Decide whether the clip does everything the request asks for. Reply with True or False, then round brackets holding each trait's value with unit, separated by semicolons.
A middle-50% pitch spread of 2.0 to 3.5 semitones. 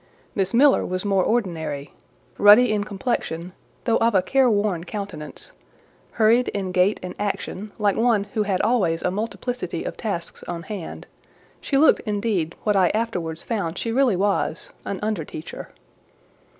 False (3.9 semitones)